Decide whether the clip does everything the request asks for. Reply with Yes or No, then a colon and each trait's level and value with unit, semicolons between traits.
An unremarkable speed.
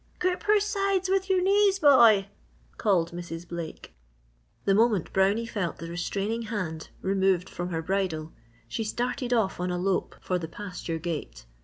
Yes: average, 160 wpm